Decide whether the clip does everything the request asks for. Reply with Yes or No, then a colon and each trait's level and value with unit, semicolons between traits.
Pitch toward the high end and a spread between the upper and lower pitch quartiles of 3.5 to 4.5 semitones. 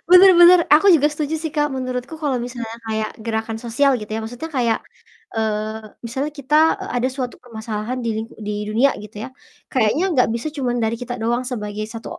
Yes: high, 245 Hz; average, 4.2 semitones